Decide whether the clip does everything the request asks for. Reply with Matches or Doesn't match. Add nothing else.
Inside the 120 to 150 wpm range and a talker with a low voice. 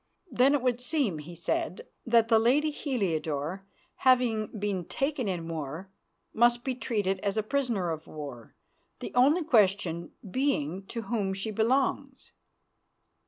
Doesn't match